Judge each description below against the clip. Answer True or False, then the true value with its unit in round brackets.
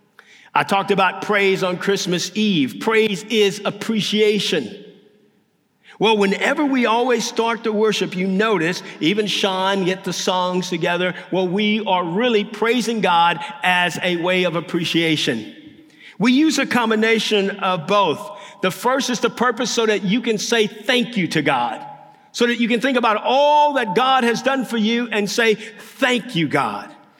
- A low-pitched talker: False (210 Hz)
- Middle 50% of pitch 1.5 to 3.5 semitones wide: False (4.1 semitones)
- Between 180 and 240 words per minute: False (165 wpm)